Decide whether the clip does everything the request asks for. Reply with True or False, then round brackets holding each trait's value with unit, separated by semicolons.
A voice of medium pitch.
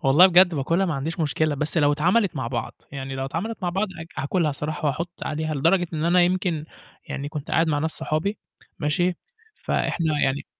True (155 Hz)